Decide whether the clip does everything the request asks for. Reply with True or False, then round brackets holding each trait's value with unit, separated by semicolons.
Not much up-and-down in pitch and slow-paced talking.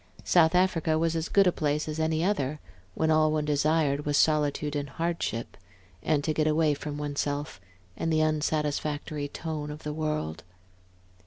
False (1.4 semitones; 170 wpm)